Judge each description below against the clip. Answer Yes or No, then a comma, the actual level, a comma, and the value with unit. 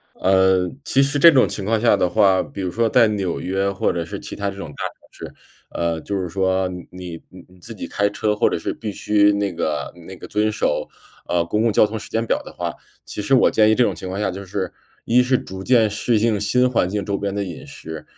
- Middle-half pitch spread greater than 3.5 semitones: No, average, 2.9 semitones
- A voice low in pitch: Yes, low, 100 Hz